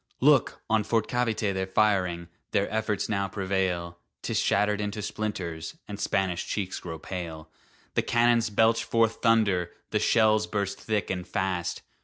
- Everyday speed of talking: Yes, average, 150 wpm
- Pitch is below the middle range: Yes, low, 100 Hz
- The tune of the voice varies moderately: Yes, average, 3.1 semitones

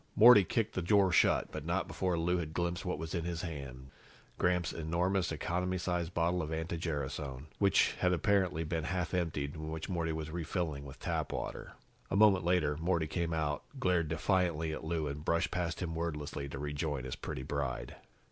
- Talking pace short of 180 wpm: No, average, 190 wpm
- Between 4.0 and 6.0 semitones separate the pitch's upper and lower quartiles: No, average, 2.8 semitones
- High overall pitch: No, very low, 85 Hz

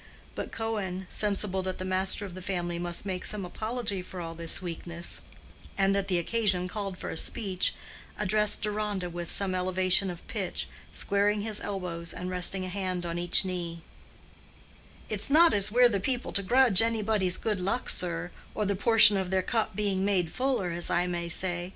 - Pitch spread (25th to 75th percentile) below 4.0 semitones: Yes, average, 2.7 semitones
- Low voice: No, high, 190 Hz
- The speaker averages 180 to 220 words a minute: Yes, average, 185 wpm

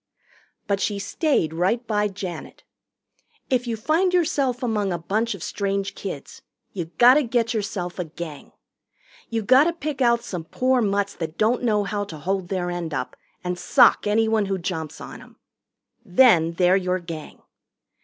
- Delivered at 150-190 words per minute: Yes, average, 165 wpm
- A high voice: Yes, high, 200 Hz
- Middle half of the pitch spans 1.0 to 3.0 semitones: No, average, 4.9 semitones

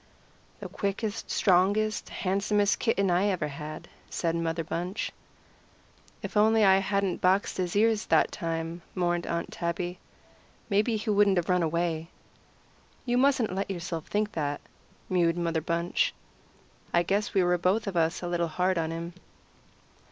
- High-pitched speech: No, medium, 180 Hz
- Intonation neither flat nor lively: Yes, average, 3.2 semitones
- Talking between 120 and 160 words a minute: Yes, average, 150 wpm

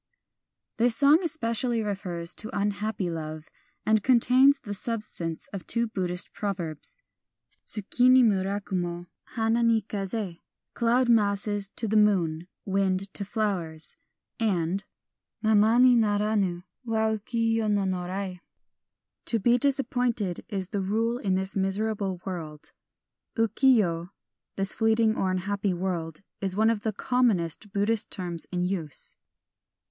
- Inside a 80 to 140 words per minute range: Yes, slow, 135 wpm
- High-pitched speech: Yes, high, 205 Hz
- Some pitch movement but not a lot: Yes, average, 3.5 semitones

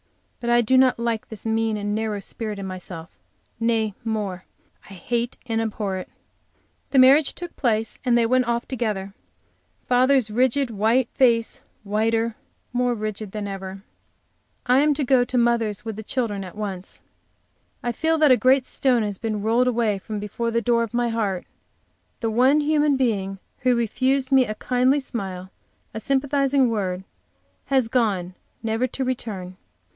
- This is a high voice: Yes, high, 230 Hz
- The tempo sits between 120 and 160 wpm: No, average, 170 wpm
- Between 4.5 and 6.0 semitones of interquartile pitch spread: No, average, 3.4 semitones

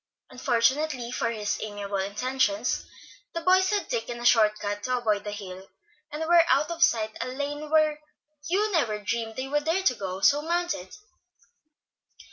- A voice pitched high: Yes, very high, 250 Hz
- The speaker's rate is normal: Yes, average, 170 wpm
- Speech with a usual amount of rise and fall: No, wide, 6.6 semitones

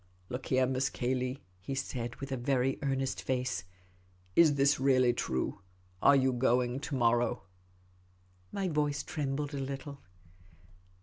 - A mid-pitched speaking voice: No, low, 130 Hz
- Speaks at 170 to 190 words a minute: No, average, 150 wpm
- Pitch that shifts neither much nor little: No, narrow, 2.2 semitones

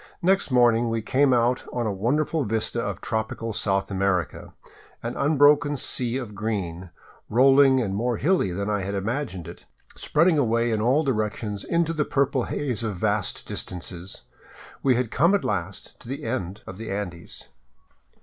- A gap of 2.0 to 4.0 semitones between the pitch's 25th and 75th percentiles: No, average, 5.0 semitones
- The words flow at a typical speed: Yes, average, 165 wpm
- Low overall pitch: Yes, low, 115 Hz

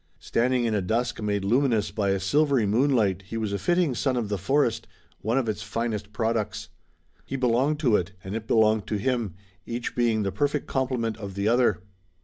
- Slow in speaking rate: No, average, 195 wpm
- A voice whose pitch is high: No, low, 115 Hz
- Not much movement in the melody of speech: No, average, 3.5 semitones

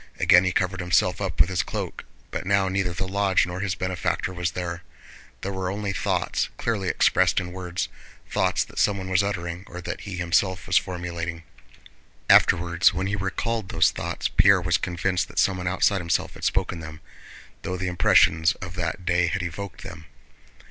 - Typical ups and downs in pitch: No, narrow, 1.8 semitones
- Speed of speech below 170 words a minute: No, average, 180 wpm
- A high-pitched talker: No, very low, 90 Hz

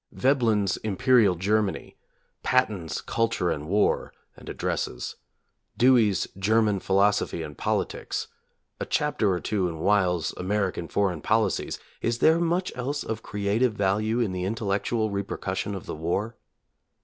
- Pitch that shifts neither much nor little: Yes, average, 3.4 semitones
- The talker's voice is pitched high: No, low, 105 Hz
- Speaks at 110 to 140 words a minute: Yes, slow, 135 wpm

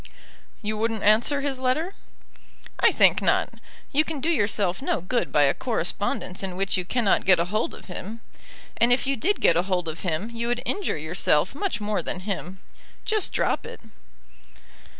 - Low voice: No, high, 215 Hz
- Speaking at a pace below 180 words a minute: No, average, 185 wpm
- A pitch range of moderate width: No, wide, 5.8 semitones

